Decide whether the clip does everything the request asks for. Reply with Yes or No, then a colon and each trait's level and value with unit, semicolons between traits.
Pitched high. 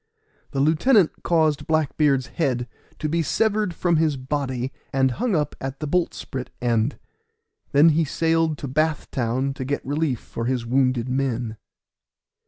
No: medium, 140 Hz